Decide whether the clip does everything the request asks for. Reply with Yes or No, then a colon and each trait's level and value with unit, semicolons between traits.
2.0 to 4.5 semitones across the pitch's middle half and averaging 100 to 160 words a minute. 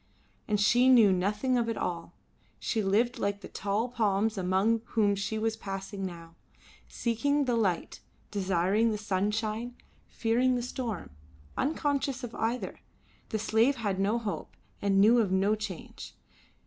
Yes: average, 3.1 semitones; average, 150 wpm